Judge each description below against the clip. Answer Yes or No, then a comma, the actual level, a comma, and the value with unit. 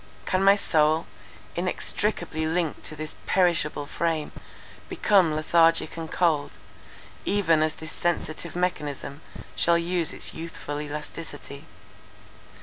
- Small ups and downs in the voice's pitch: Yes, narrow, 2.2 semitones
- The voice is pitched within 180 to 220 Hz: No, medium, 165 Hz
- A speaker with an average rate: No, slow, 110 wpm